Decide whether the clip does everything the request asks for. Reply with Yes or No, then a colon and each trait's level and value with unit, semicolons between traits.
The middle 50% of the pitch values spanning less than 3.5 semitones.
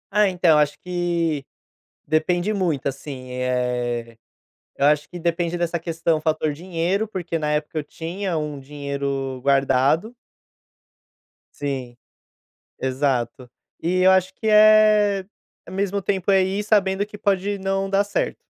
No: wide, 5.4 semitones